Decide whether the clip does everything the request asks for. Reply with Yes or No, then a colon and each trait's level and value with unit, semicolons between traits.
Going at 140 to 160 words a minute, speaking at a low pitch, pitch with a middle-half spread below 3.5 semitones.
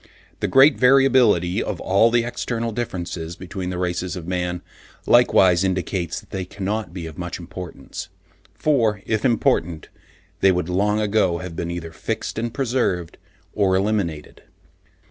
No: average, 145 wpm; very low, 95 Hz; average, 4.2 semitones